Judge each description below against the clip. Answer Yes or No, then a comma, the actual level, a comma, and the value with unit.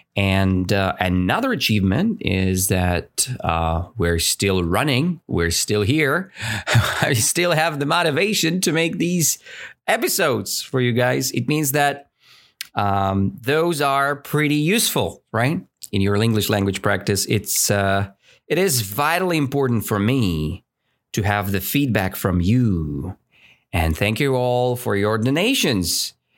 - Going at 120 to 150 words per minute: Yes, slow, 135 wpm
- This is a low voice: Yes, low, 110 Hz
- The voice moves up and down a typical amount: No, wide, 6.7 semitones